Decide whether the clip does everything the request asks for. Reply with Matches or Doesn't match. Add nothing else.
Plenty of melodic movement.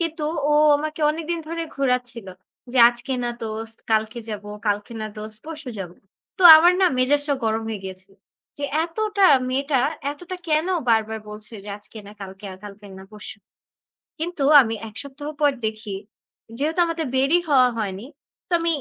Matches